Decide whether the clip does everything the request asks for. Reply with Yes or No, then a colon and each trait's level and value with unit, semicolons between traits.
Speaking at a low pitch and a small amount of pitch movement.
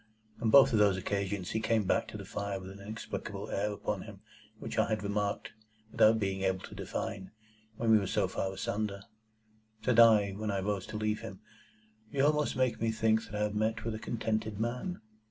Yes: low, 105 Hz; narrow, 2.0 semitones